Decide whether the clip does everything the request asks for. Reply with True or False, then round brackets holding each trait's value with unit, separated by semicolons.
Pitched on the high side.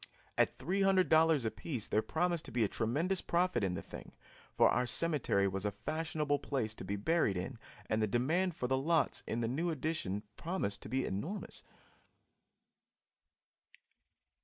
False (135 Hz)